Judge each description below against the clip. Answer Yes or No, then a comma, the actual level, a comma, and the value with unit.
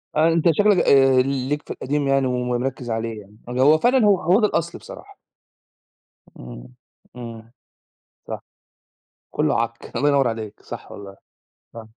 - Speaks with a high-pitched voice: No, low, 130 Hz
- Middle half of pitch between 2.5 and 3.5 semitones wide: No, average, 4.5 semitones